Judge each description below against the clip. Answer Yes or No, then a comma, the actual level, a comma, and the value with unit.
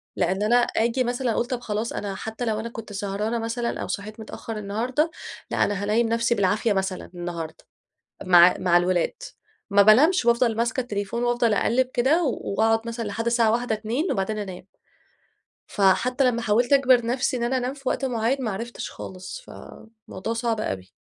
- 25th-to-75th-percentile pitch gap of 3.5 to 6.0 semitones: No, average, 3.1 semitones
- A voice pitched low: No, high, 225 Hz